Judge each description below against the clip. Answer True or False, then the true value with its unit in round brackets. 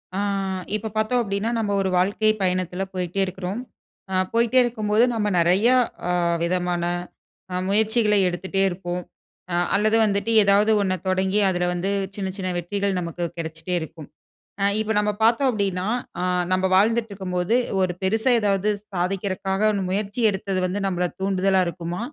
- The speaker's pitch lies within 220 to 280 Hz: False (195 Hz)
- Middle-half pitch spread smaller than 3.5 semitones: True (2.7 semitones)